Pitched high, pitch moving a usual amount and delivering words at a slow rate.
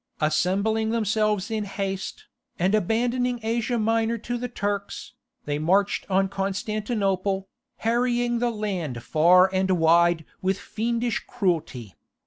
Yes: high, 205 Hz; average, 3.5 semitones; slow, 115 wpm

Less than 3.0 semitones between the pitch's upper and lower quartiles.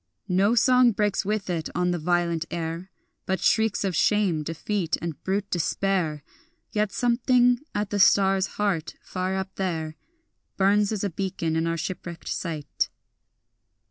No: average, 3.7 semitones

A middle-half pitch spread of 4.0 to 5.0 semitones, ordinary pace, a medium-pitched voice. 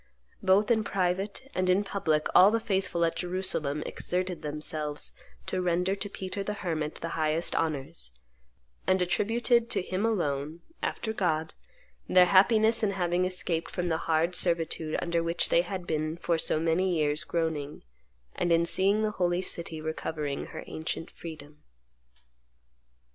No: average, 3.1 semitones; average, 150 wpm; medium, 175 Hz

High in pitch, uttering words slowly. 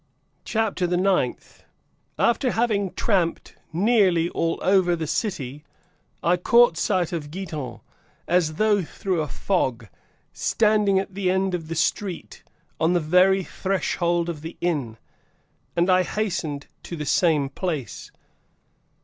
No: medium, 175 Hz; slow, 130 wpm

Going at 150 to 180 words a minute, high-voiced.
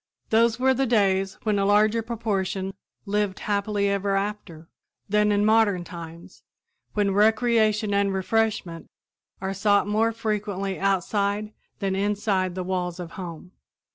No: slow, 135 wpm; high, 200 Hz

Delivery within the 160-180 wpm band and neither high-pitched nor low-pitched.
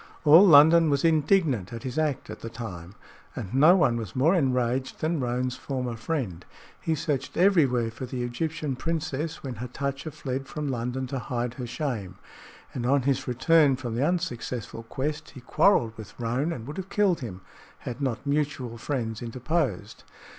No: average, 170 wpm; low, 130 Hz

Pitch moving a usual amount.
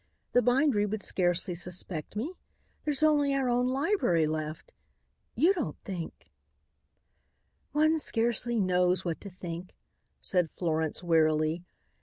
No: wide, 7.3 semitones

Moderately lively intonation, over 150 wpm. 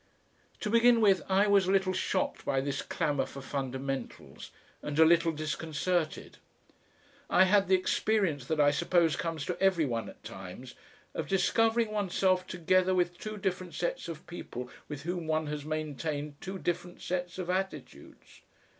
Yes: average, 4.1 semitones; average, 160 wpm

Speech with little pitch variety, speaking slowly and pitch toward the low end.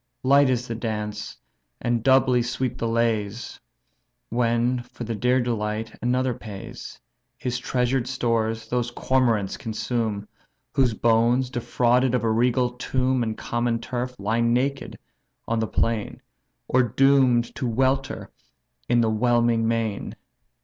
Yes: narrow, 1.9 semitones; slow, 130 wpm; low, 120 Hz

